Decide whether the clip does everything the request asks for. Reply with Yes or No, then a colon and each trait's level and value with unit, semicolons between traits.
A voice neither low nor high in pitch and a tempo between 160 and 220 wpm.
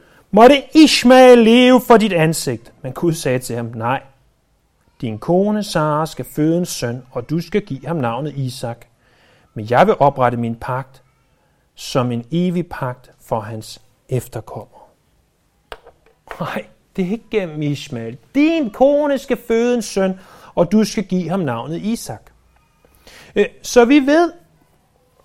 No: medium, 160 Hz; slow, 145 wpm